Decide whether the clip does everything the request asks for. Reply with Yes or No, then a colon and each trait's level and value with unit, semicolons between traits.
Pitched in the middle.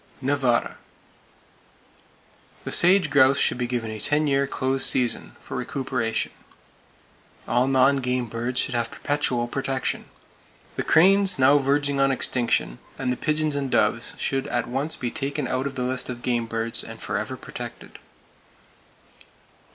No: low, 130 Hz